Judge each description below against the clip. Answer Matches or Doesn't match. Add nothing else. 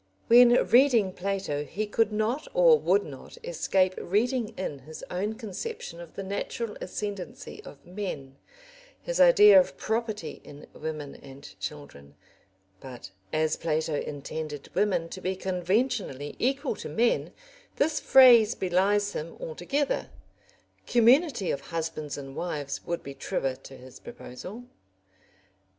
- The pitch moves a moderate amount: Doesn't match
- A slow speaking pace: Matches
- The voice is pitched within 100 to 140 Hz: Doesn't match